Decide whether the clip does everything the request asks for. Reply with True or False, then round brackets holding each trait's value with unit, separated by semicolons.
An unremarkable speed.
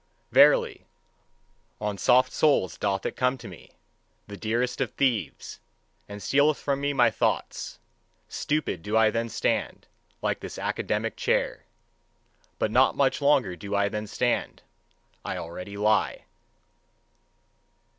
False (130 wpm)